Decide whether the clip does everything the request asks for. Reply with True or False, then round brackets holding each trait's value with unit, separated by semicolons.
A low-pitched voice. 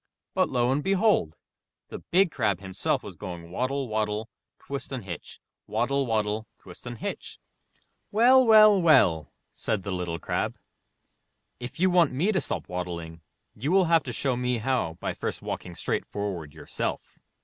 True (120 Hz)